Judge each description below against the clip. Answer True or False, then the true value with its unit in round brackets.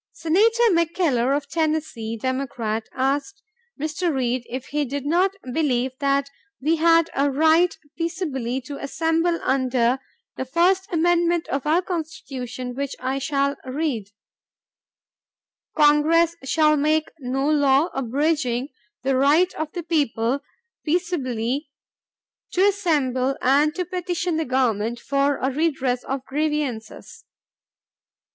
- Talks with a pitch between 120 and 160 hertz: False (285 Hz)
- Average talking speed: False (120 wpm)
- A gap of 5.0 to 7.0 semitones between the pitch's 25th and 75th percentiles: False (4.1 semitones)